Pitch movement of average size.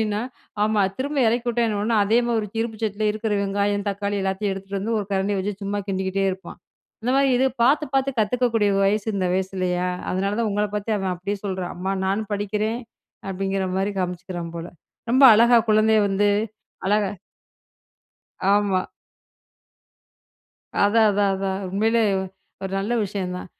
No: narrow, 2.3 semitones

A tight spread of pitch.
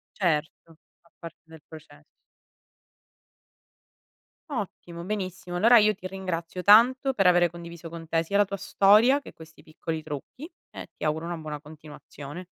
No: average, 3.8 semitones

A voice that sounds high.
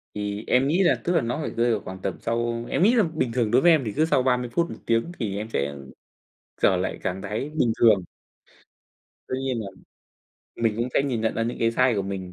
No: low, 115 Hz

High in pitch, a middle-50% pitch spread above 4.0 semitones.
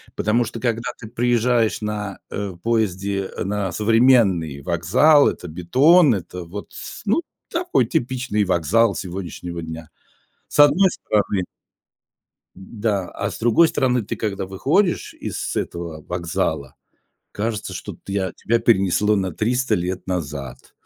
No: low, 105 Hz; average, 4.6 semitones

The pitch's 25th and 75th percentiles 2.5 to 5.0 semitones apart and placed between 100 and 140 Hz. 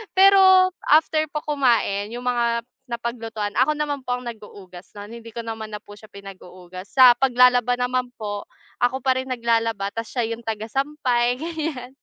No: average, 3.2 semitones; high, 240 Hz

